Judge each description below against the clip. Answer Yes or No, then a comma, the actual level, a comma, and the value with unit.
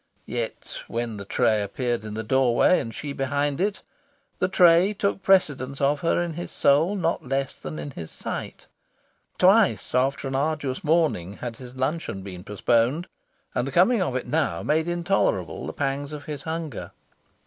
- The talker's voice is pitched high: No, medium, 140 Hz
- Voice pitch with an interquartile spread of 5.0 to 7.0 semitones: Yes, wide, 5.5 semitones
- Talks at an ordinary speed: Yes, average, 170 wpm